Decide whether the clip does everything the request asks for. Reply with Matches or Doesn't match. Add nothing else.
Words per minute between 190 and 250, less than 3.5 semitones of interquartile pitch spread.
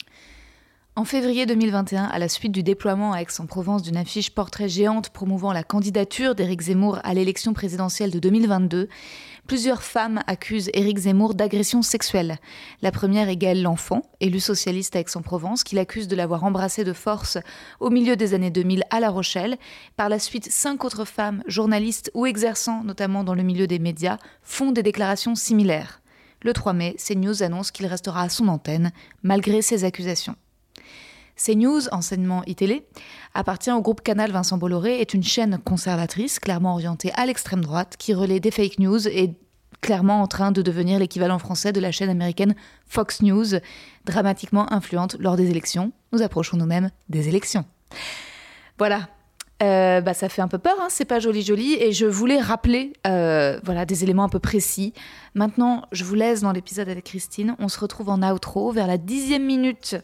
Doesn't match